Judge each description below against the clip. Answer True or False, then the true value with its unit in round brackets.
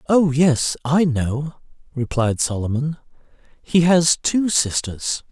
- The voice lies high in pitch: False (145 Hz)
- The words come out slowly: True (115 wpm)